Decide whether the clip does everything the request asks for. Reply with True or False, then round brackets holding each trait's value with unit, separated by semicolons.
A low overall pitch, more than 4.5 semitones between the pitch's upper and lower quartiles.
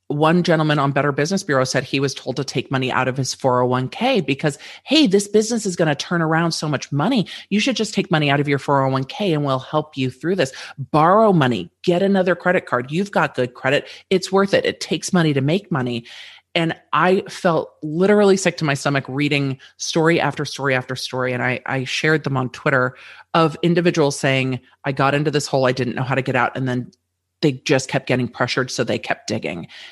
False (145 Hz; 4.9 semitones)